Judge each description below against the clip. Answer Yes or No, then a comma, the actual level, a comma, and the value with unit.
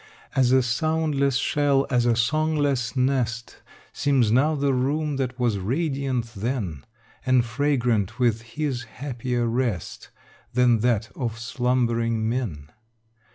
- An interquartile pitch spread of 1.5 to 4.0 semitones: Yes, average, 3.0 semitones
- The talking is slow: Yes, slow, 120 wpm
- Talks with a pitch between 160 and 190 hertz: No, low, 125 Hz